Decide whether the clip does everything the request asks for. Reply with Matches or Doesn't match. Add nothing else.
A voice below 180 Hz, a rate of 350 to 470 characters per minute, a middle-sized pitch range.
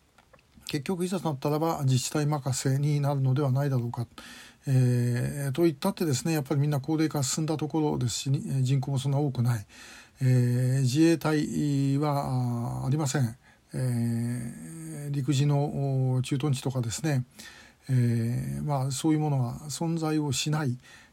Doesn't match